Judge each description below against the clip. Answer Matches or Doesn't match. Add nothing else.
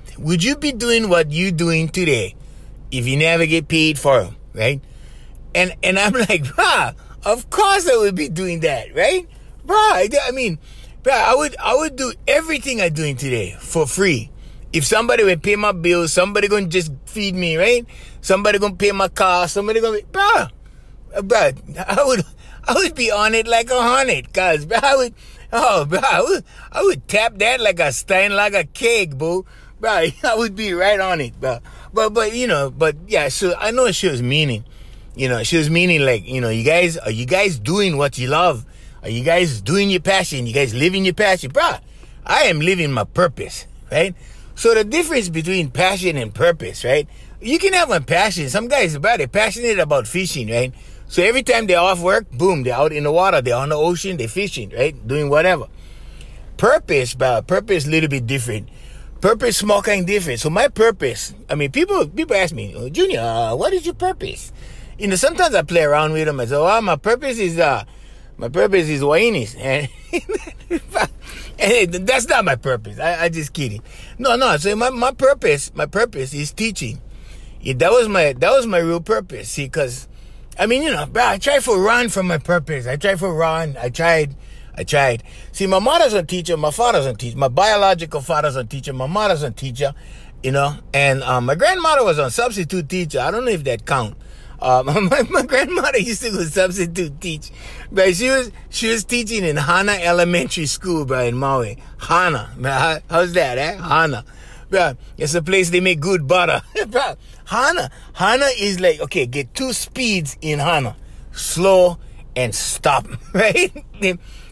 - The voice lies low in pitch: Doesn't match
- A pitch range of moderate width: Doesn't match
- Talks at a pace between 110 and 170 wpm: Doesn't match